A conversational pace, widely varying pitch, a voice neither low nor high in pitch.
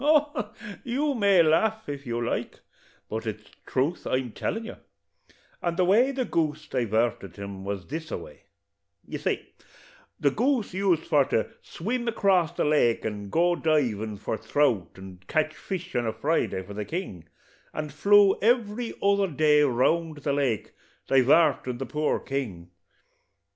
Yes: average, 160 wpm; wide, 8.9 semitones; medium, 150 Hz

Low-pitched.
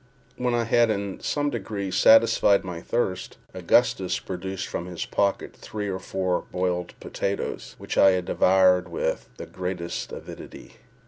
Yes: very low, 95 Hz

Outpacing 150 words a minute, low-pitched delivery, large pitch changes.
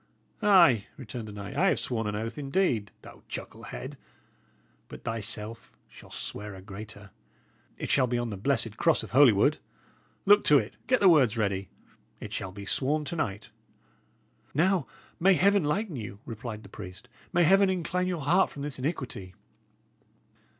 Yes: average, 165 wpm; low, 125 Hz; wide, 8.3 semitones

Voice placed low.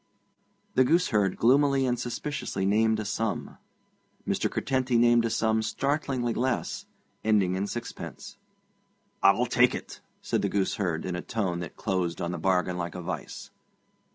Yes: low, 110 Hz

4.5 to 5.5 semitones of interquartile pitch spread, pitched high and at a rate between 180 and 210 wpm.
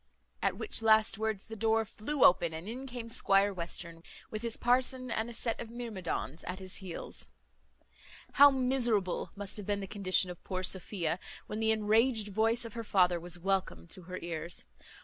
No: average, 3.8 semitones; high, 210 Hz; average, 185 wpm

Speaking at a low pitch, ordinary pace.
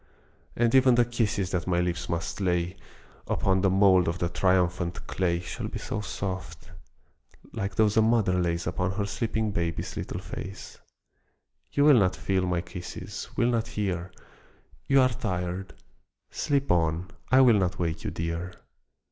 Yes: very low, 95 Hz; average, 160 wpm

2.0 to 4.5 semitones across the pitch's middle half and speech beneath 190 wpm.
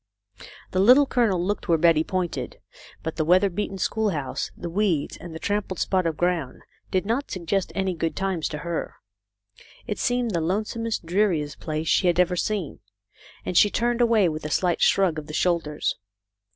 Yes: average, 4.1 semitones; average, 180 wpm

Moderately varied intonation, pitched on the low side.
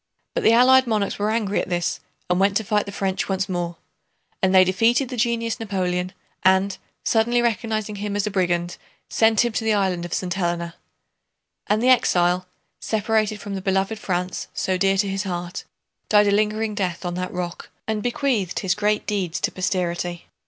No: average, 3.1 semitones; high, 200 Hz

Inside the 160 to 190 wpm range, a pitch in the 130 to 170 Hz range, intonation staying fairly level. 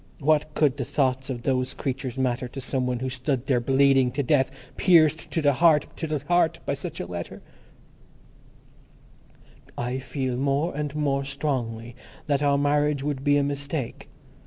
Yes: average, 170 wpm; medium, 140 Hz; narrow, 2.3 semitones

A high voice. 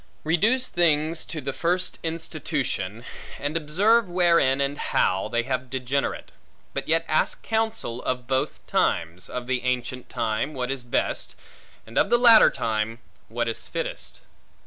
No: low, 135 Hz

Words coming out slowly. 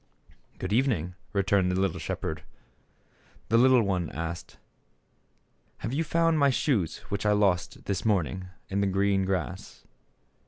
No: average, 145 wpm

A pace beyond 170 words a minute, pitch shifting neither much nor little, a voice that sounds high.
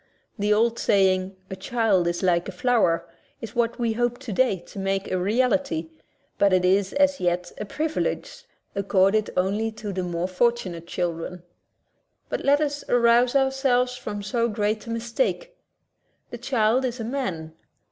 No: average, 155 wpm; average, 4.7 semitones; high, 215 Hz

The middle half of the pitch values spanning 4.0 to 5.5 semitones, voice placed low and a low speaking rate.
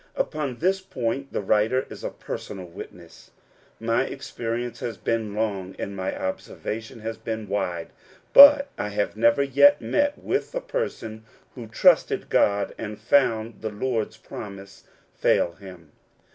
No: average, 4.4 semitones; low, 110 Hz; average, 145 wpm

